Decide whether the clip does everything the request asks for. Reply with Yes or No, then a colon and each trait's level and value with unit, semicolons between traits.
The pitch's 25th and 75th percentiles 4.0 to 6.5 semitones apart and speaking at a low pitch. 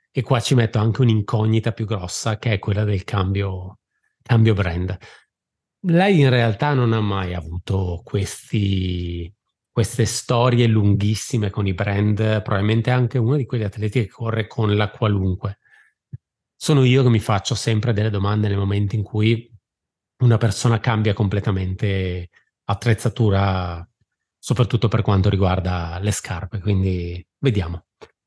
No: average, 2.9 semitones; low, 105 Hz